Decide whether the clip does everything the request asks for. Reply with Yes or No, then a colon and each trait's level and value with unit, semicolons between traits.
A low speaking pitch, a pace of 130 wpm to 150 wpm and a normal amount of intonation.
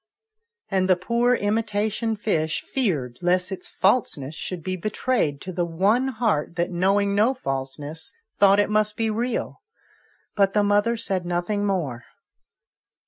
No: high, 195 Hz; average, 140 wpm; average, 3.8 semitones